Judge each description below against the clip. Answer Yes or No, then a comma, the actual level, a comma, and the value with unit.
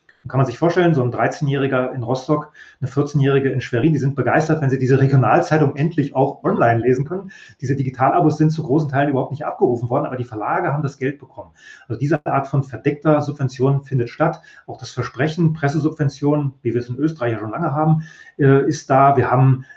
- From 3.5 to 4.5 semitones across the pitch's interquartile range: No, average, 2.9 semitones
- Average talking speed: No, fast, 205 wpm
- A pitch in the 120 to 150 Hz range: Yes, medium, 140 Hz